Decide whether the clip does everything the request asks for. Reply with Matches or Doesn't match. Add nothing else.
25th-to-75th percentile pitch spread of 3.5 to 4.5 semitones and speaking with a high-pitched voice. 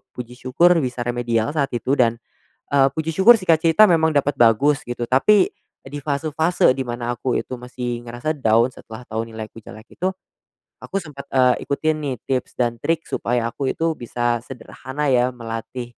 Doesn't match